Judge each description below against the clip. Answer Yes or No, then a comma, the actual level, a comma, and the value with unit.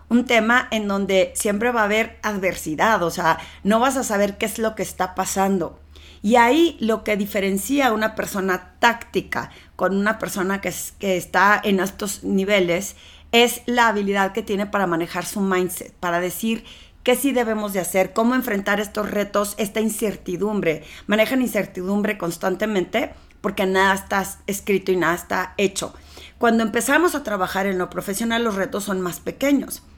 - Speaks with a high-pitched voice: Yes, high, 205 Hz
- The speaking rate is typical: Yes, average, 170 wpm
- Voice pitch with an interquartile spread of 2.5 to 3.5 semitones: Yes, average, 3.1 semitones